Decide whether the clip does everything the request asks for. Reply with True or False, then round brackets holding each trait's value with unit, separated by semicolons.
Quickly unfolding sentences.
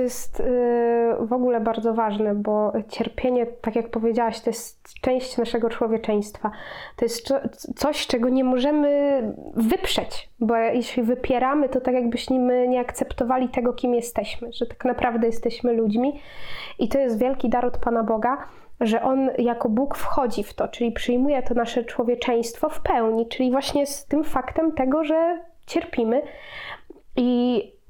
False (150 wpm)